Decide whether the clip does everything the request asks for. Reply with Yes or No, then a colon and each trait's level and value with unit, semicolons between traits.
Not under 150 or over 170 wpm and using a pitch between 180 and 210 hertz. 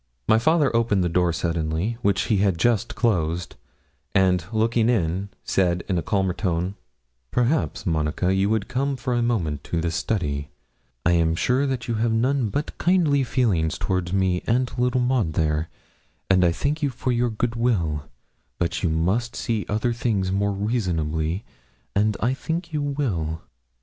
No: average, 165 wpm; low, 100 Hz